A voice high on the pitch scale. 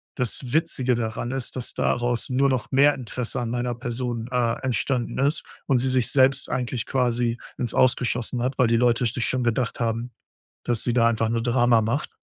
No: low, 125 Hz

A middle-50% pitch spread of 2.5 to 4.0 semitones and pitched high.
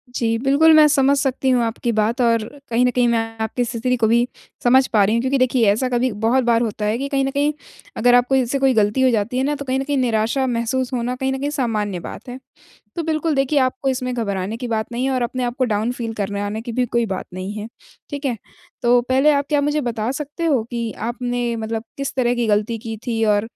Yes: average, 2.9 semitones; high, 245 Hz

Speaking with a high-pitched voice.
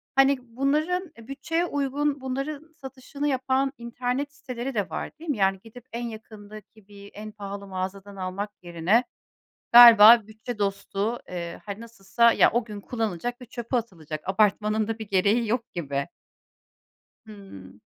Yes: high, 225 Hz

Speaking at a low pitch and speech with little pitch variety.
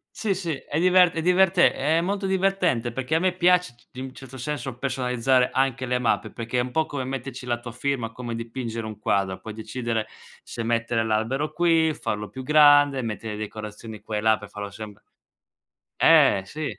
No: low, 125 Hz; average, 5.2 semitones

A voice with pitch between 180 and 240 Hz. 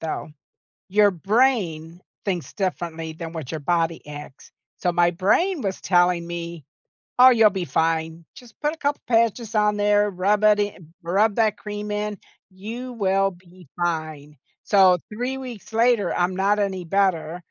Yes: high, 190 Hz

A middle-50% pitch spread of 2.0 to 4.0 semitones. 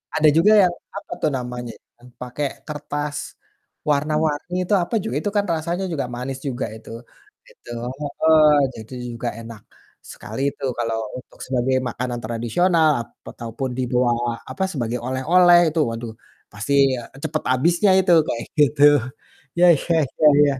No: average, 4.7 semitones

